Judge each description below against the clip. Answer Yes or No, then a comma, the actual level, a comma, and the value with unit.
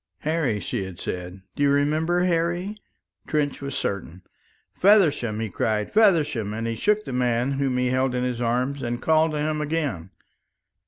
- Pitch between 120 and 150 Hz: Yes, low, 135 Hz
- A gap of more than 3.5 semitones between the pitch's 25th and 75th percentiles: Yes, wide, 5.5 semitones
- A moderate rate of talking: Yes, average, 170 wpm